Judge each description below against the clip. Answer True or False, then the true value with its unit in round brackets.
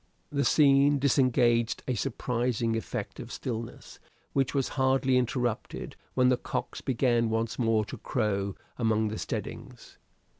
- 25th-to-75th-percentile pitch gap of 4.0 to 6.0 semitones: False (2.8 semitones)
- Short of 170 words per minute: True (135 wpm)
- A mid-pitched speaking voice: False (120 Hz)